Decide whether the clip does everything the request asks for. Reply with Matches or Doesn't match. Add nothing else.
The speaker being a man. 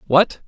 Matches